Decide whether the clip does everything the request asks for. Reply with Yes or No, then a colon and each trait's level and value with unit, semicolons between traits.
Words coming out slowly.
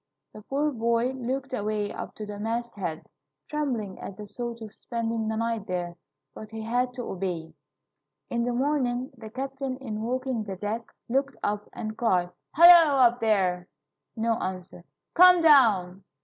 No: average, 160 wpm